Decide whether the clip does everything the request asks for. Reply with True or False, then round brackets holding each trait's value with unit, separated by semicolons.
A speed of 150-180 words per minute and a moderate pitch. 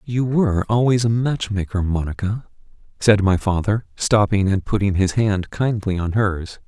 False (160 wpm; 105 Hz)